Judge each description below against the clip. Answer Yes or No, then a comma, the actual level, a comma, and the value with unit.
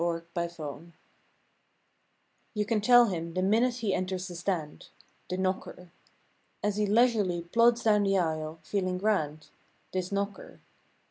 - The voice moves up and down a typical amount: Yes, average, 3.6 semitones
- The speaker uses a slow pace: Yes, slow, 130 wpm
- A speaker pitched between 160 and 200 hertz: Yes, medium, 185 Hz